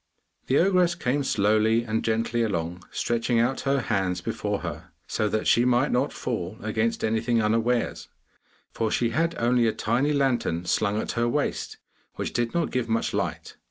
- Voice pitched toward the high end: No, low, 115 Hz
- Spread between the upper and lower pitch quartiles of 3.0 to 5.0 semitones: No, narrow, 2.6 semitones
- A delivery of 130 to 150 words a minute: No, average, 170 wpm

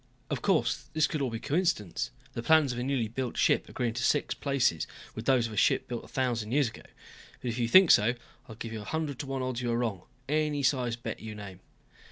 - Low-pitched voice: Yes, low, 125 Hz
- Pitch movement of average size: Yes, average, 3.5 semitones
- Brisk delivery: Yes, fast, 245 wpm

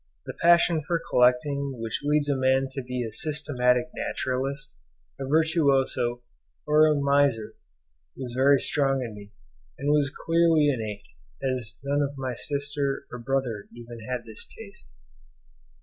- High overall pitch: No, low, 135 Hz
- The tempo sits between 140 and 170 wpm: Yes, average, 145 wpm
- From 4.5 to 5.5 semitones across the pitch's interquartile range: No, average, 2.8 semitones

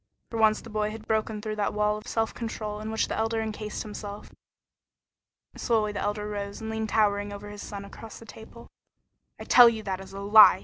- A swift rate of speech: Yes, fast, 215 wpm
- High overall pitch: Yes, high, 215 Hz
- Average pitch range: No, narrow, 1.2 semitones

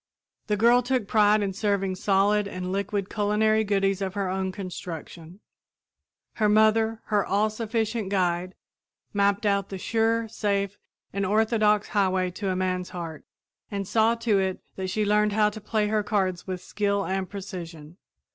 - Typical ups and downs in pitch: No, narrow, 2.2 semitones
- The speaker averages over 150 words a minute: Yes, average, 160 wpm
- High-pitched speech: Yes, high, 200 Hz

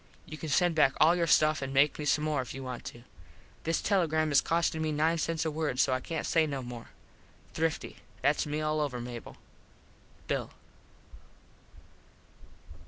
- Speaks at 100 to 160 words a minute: No, average, 180 wpm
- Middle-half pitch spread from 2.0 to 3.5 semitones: Yes, average, 2.9 semitones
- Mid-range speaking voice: Yes, medium, 155 Hz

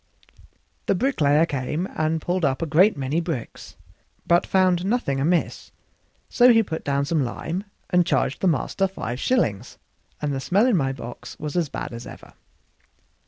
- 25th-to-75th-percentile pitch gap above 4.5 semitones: Yes, average, 5.0 semitones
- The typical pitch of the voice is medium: Yes, medium, 165 Hz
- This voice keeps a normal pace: Yes, average, 165 wpm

